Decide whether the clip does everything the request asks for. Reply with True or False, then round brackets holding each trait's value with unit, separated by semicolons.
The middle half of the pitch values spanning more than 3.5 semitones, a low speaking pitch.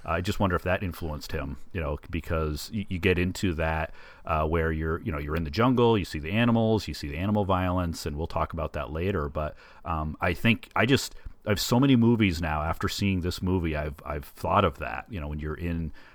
True (4.2 semitones; 85 Hz)